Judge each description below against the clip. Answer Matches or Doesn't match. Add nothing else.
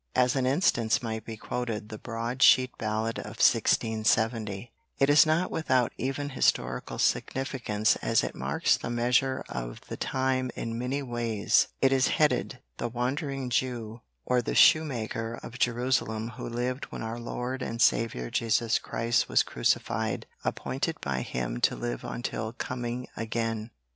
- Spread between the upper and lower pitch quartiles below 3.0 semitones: Matches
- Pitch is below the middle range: Matches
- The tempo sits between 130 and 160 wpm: Matches